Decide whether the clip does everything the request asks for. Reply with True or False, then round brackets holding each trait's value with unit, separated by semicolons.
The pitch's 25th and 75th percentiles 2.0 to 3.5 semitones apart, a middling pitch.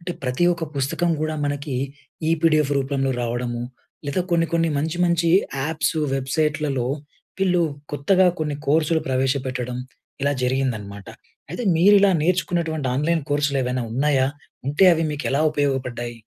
False (3.9 semitones; 145 Hz)